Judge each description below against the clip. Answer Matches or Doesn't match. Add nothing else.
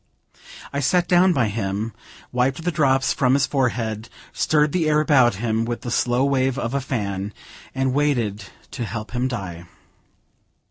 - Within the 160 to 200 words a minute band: Matches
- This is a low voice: Matches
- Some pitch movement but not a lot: Matches